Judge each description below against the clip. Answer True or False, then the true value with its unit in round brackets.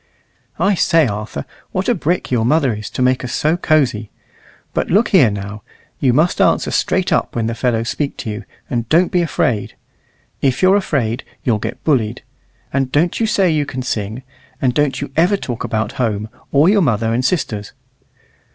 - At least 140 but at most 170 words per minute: False (190 wpm)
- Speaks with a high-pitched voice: False (130 Hz)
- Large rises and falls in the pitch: True (6.3 semitones)